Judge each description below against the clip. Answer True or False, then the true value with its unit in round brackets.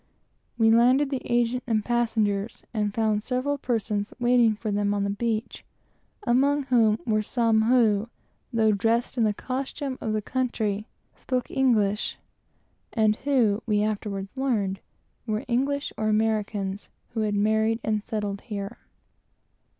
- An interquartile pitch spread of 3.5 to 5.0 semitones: False (2.7 semitones)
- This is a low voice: False (220 Hz)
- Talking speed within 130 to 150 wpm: True (145 wpm)